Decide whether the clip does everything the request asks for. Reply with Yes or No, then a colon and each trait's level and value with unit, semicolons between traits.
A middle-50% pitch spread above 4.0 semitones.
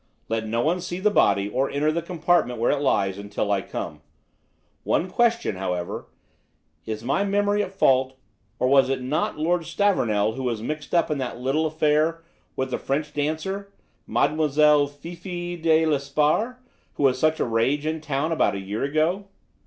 Yes: average, 4.7 semitones